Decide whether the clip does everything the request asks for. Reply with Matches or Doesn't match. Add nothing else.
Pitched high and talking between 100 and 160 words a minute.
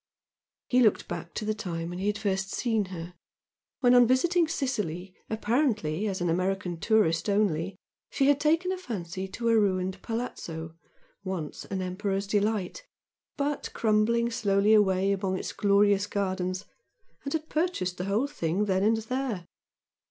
Matches